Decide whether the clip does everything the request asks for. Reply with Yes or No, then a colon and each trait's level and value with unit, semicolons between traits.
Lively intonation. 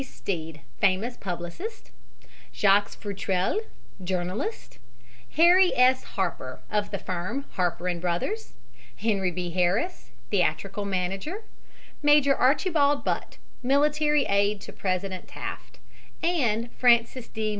Yes: wide, 7.4 semitones